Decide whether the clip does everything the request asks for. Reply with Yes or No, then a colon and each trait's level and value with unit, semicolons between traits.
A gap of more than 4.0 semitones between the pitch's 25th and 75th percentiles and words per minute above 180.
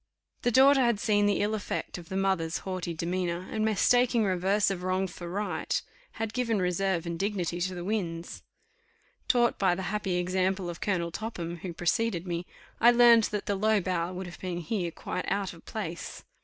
No: average, 3.4 semitones; average, 190 wpm